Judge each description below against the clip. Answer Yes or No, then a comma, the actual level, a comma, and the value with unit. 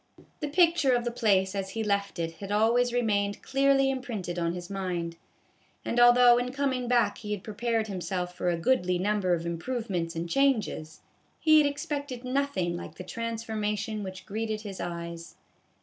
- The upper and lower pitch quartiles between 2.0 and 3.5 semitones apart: No, average, 5.2 semitones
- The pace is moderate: Yes, average, 180 wpm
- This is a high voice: Yes, high, 210 Hz